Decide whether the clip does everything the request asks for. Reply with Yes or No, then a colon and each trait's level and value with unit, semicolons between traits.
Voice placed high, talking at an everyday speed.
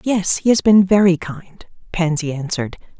No: medium, 180 Hz; average, 160 wpm